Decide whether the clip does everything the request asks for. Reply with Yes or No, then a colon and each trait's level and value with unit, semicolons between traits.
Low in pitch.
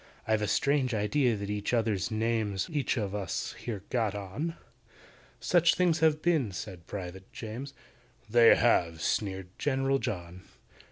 Yes: low, 110 Hz